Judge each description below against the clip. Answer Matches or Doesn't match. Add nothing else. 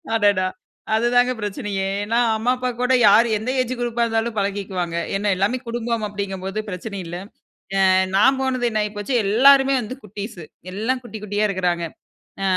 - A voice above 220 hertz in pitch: Doesn't match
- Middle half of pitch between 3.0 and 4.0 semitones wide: Matches